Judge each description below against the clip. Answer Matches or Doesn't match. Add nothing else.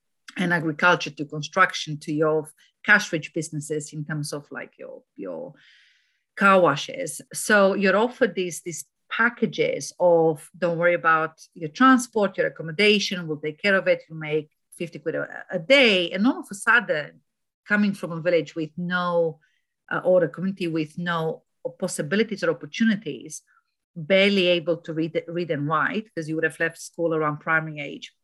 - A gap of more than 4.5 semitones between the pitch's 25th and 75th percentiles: Doesn't match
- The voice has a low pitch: Doesn't match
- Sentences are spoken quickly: Doesn't match